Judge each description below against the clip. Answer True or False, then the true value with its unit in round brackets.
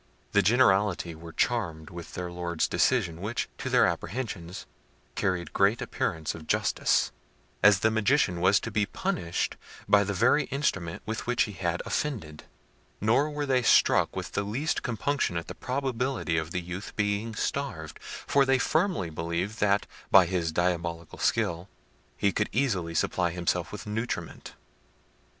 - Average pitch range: False (5.8 semitones)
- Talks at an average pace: True (155 wpm)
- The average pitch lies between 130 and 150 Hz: False (100 Hz)